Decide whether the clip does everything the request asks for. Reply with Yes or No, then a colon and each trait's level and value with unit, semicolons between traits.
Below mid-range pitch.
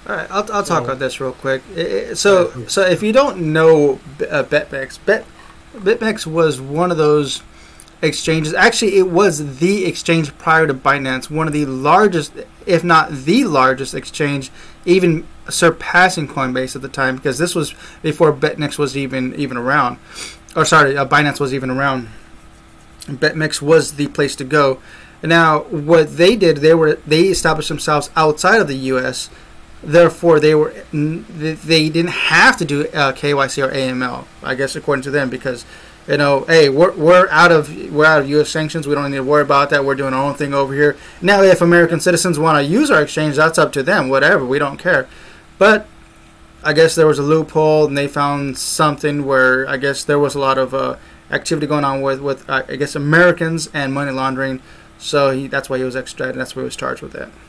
No: medium, 150 Hz